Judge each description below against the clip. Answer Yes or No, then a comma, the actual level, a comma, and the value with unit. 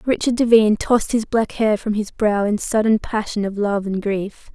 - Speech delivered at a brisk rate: Yes, fast, 210 wpm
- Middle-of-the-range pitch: No, high, 215 Hz